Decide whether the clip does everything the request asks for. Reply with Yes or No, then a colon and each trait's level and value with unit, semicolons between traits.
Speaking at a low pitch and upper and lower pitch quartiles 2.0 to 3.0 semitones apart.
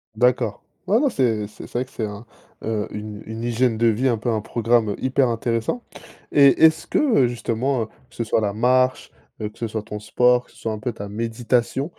Yes: low, 115 Hz; narrow, 2.5 semitones